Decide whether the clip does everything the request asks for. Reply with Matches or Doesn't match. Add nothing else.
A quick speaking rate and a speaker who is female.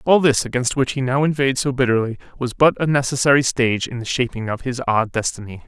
Doesn't match